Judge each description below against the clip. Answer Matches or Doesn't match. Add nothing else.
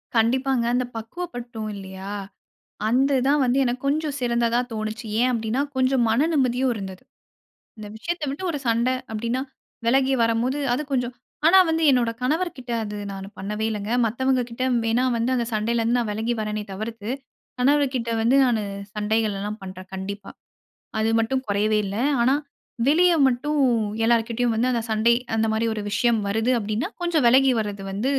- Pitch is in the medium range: Doesn't match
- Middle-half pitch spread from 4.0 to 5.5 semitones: Doesn't match